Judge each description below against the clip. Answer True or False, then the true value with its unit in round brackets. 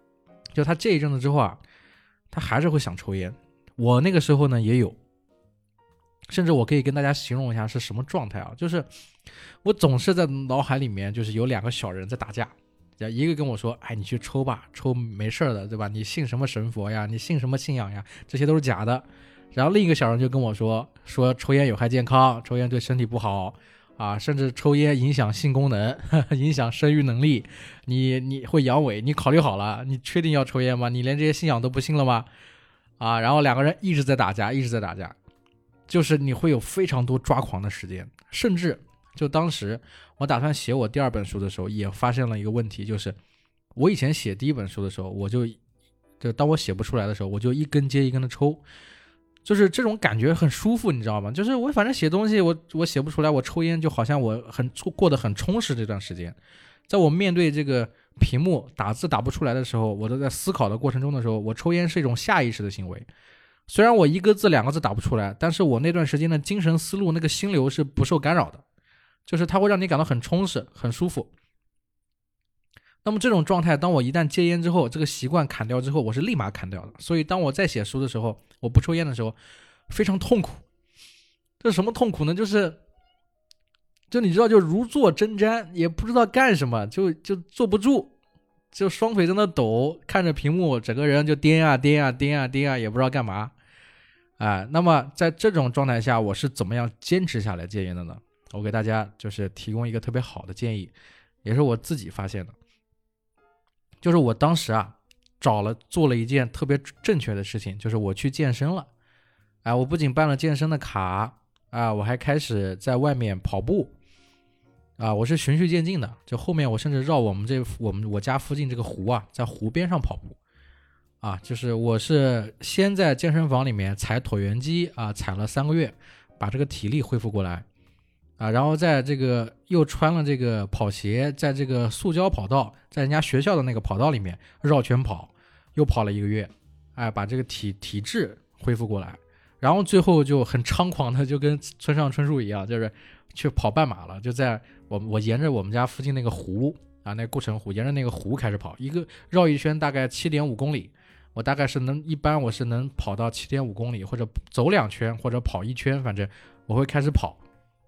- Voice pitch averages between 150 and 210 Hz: False (130 Hz)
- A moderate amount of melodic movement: False (5.8 semitones)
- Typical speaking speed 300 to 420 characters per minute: True (310 characters per minute)